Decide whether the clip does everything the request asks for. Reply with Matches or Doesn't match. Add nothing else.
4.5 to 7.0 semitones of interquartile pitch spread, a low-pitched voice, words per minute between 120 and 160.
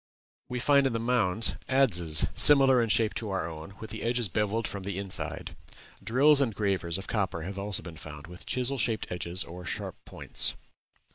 Doesn't match